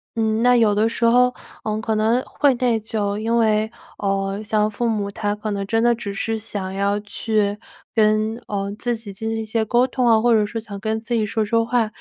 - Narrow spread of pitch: Yes, narrow, 1.8 semitones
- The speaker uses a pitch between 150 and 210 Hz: No, high, 220 Hz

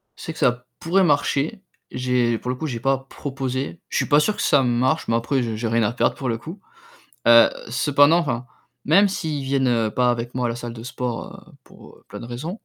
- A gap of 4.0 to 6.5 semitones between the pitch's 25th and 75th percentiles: No, average, 3.6 semitones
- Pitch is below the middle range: Yes, low, 130 Hz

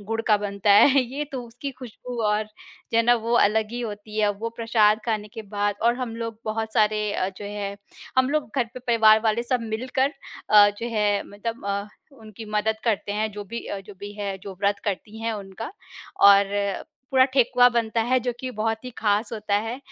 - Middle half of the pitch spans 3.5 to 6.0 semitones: No, narrow, 2.4 semitones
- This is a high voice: Yes, high, 220 Hz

